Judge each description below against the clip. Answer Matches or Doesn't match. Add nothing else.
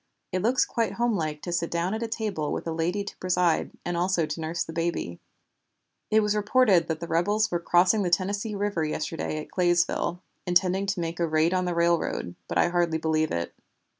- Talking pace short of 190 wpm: Doesn't match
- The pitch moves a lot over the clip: Doesn't match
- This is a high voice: Doesn't match